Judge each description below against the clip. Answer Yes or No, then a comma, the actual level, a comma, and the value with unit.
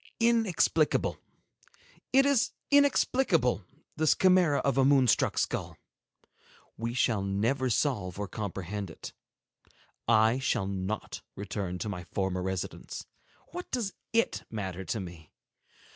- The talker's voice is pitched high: No, low, 115 Hz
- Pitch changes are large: Yes, wide, 8.3 semitones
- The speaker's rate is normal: No, slow, 120 wpm